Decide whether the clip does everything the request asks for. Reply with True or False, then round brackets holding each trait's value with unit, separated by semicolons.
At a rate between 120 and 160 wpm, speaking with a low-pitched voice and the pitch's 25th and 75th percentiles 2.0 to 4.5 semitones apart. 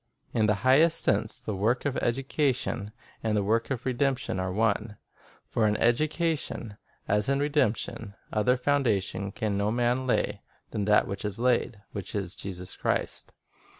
True (150 wpm; 115 Hz; 4.0 semitones)